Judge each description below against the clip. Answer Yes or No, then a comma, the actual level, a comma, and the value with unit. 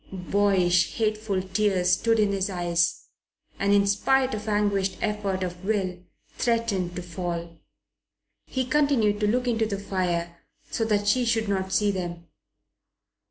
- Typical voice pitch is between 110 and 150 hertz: No, high, 200 Hz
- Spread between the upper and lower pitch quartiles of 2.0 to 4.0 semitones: Yes, average, 3.0 semitones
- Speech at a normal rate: Yes, average, 145 wpm